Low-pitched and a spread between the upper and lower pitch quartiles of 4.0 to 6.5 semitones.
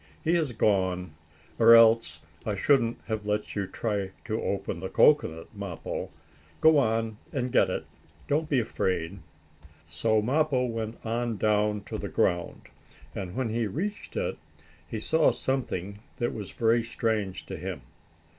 No: low, 110 Hz; average, 3.3 semitones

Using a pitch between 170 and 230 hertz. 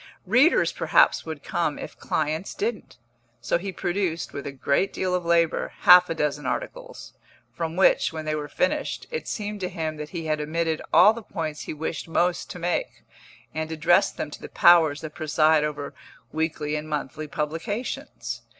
No: medium, 160 Hz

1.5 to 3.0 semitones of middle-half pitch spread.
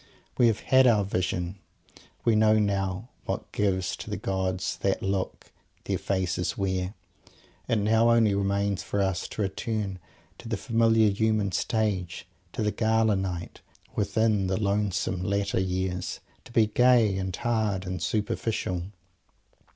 Yes: average, 2.7 semitones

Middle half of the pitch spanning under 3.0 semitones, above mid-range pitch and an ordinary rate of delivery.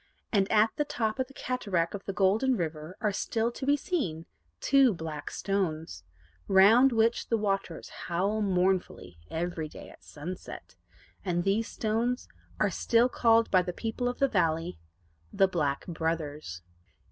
No: wide, 5.6 semitones; high, 195 Hz; average, 155 wpm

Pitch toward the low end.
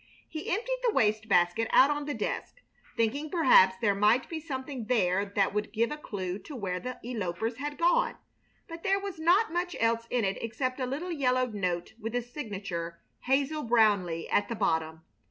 No: high, 235 Hz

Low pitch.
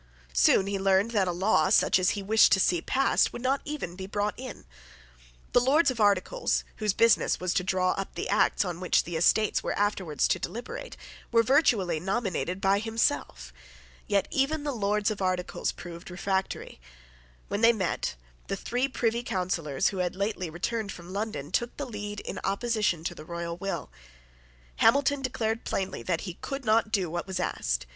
No: high, 200 Hz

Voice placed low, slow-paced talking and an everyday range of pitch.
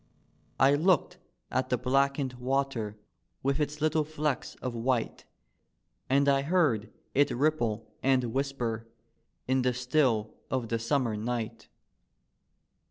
Yes: low, 130 Hz; slow, 120 wpm; average, 3.1 semitones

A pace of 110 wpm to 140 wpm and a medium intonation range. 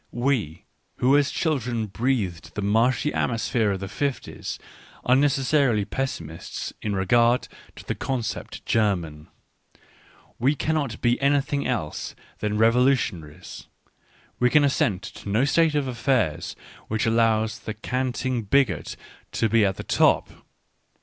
Yes: slow, 135 wpm; average, 4.4 semitones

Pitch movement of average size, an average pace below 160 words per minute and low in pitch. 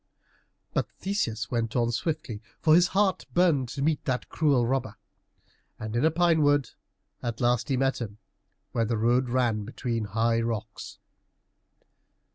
Yes: average, 4.5 semitones; average, 150 wpm; low, 125 Hz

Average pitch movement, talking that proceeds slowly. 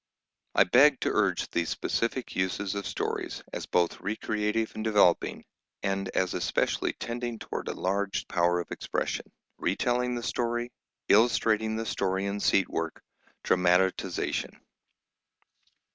Yes: average, 3.7 semitones; slow, 125 wpm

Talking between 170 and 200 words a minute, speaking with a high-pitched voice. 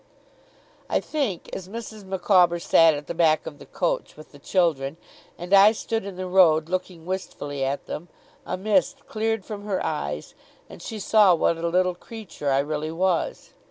No: average, 180 wpm; medium, 180 Hz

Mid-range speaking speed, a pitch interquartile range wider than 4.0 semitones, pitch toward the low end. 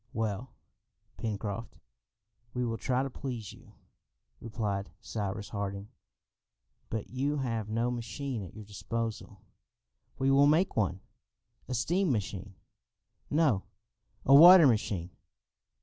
No: slow, 115 wpm; average, 4.5 semitones; low, 115 Hz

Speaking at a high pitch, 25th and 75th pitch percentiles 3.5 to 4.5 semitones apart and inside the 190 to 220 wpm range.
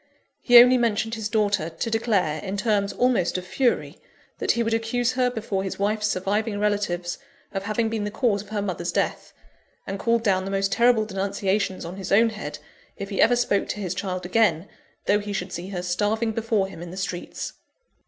No: high, 205 Hz; average, 2.8 semitones; fast, 205 wpm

